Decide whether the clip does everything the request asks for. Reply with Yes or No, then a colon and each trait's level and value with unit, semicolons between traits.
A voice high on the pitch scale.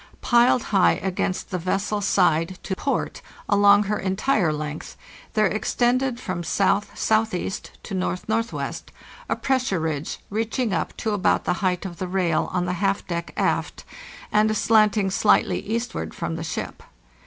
Yes: high, 195 Hz